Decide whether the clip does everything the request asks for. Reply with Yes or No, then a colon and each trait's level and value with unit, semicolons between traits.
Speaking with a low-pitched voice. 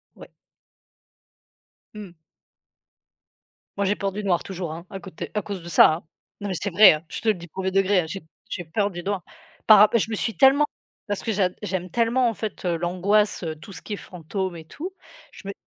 No: high, 195 Hz